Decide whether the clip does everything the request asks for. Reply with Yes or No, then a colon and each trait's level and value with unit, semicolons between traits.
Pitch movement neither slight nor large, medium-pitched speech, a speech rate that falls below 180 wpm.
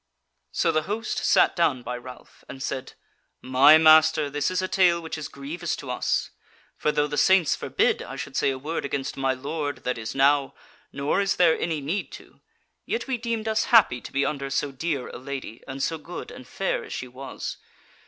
No: average, 4.1 semitones; medium, 145 Hz; fast, 205 wpm